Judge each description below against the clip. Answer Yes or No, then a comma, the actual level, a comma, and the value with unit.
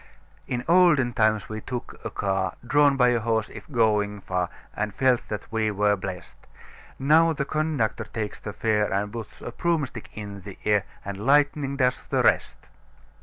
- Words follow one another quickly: No, average, 170 wpm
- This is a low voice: Yes, low, 110 Hz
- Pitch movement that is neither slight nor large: Yes, average, 4.8 semitones